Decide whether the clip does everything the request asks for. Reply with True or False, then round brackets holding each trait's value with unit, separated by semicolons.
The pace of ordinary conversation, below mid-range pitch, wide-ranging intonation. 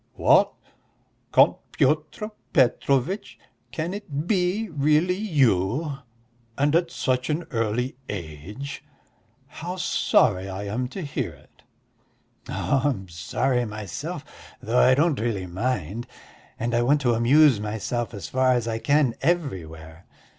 False (130 wpm; 130 Hz; 6.0 semitones)